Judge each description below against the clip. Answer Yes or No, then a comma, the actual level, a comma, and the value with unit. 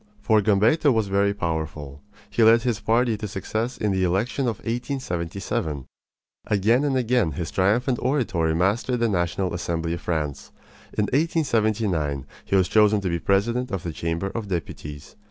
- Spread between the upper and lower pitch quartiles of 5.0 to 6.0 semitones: Yes, wide, 5.5 semitones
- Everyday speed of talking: Yes, average, 160 wpm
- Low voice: Yes, low, 100 Hz